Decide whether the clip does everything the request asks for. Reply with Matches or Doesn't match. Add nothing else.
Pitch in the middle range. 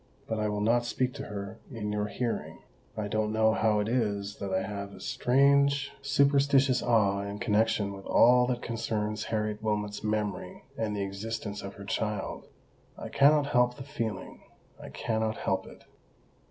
Doesn't match